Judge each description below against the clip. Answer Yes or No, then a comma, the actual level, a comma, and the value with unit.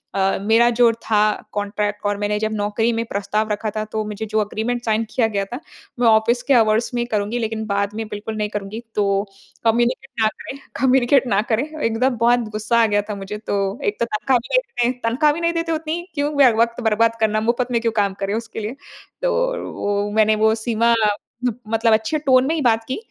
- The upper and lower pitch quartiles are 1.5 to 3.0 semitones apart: Yes, narrow, 2.5 semitones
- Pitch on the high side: Yes, high, 225 Hz